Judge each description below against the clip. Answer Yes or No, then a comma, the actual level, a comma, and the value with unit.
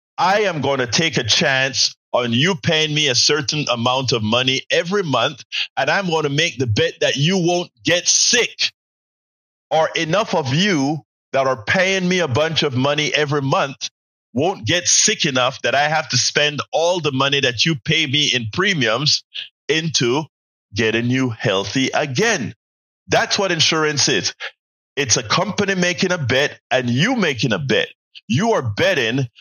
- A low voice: No, medium, 145 Hz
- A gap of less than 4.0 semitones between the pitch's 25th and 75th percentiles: No, average, 4.3 semitones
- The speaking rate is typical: Yes, average, 175 wpm